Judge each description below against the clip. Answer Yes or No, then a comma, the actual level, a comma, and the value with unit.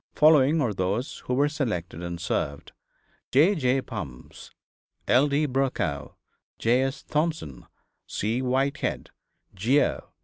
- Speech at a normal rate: No, slow, 115 wpm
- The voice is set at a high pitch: No, low, 130 Hz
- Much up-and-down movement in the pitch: Yes, wide, 6.9 semitones